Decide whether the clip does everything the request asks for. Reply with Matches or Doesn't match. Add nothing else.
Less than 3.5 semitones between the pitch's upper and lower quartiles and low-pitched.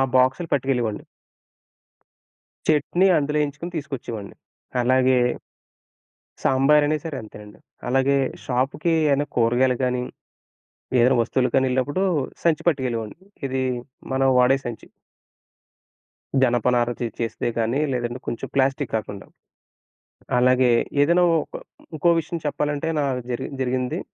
Matches